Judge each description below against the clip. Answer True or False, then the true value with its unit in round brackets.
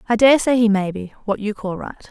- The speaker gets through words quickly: True (230 wpm)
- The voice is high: True (215 Hz)